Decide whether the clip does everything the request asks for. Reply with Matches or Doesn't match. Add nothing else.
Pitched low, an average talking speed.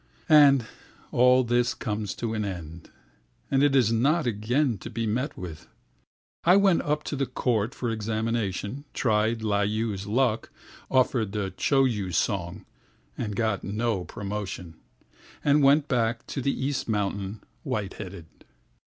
Doesn't match